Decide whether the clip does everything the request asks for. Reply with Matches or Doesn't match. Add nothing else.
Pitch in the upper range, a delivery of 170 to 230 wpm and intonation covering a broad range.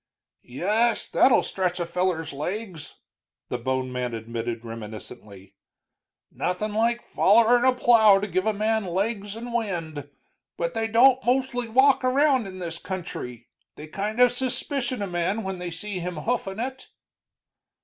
Doesn't match